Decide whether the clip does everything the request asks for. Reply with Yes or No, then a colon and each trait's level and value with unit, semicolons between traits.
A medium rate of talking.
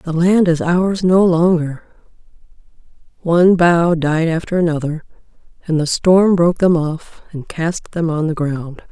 Yes: average, 155 wpm